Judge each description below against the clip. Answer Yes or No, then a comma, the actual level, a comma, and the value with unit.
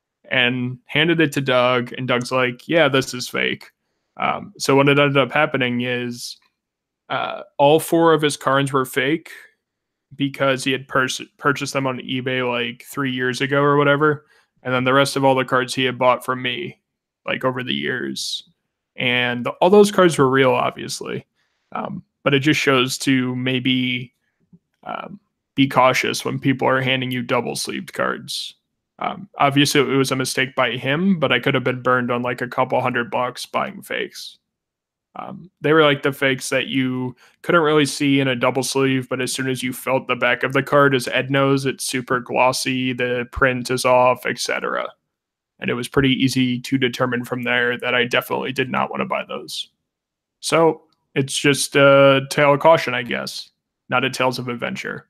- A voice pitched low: Yes, low, 130 Hz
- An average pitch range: No, narrow, 1.9 semitones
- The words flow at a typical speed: Yes, average, 190 wpm